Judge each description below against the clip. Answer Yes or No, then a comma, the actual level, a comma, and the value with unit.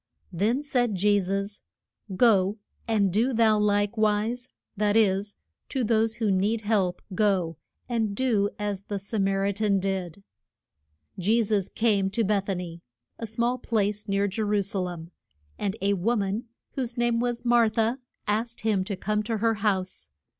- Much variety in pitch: No, narrow, 2.5 semitones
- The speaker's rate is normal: Yes, average, 170 wpm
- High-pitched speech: Yes, high, 210 Hz